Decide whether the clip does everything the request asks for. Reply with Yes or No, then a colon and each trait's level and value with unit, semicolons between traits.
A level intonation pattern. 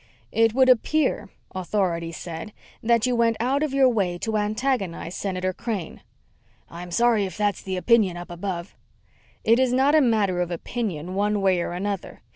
No: average, 4.7 semitones